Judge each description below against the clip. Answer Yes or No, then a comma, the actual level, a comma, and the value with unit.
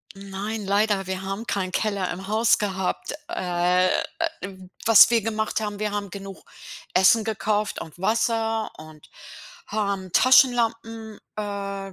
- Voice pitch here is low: No, high, 205 Hz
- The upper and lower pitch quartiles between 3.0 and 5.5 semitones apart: No, narrow, 2.5 semitones